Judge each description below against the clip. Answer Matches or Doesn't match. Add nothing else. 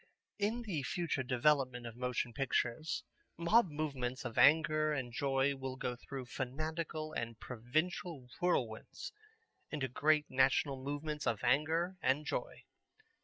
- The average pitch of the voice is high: Doesn't match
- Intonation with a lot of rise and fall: Doesn't match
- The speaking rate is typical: Doesn't match